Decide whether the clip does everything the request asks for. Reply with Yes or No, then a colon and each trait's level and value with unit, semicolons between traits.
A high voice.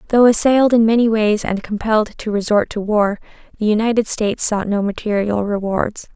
Yes: high, 215 Hz